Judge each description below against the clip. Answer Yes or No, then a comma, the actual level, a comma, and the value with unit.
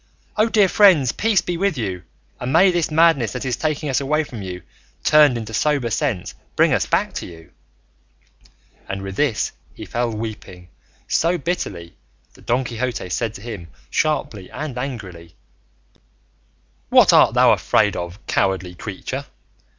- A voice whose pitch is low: Yes, low, 120 Hz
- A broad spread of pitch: Yes, wide, 7.9 semitones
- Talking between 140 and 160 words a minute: Yes, average, 155 wpm